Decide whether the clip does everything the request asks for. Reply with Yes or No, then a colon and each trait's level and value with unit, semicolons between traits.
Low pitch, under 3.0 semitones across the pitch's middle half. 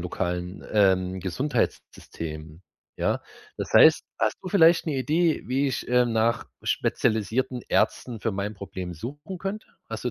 No: low, 115 Hz; wide, 7.4 semitones